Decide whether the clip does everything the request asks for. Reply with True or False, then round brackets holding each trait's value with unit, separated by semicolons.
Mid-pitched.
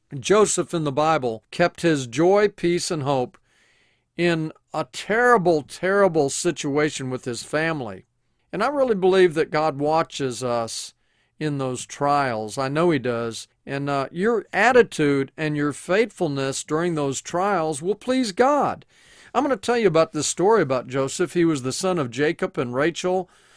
True (155 Hz)